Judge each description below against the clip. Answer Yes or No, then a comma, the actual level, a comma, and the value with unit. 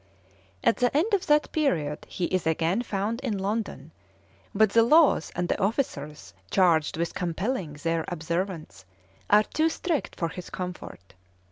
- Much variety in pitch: Yes, wide, 6.2 semitones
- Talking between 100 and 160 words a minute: Yes, average, 150 wpm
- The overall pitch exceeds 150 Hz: Yes, high, 190 Hz